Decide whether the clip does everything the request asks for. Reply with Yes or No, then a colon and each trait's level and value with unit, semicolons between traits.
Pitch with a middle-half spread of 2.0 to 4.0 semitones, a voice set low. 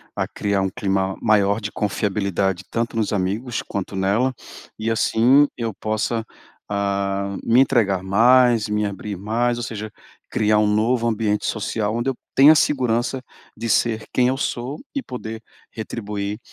Yes: average, 2.9 semitones; low, 110 Hz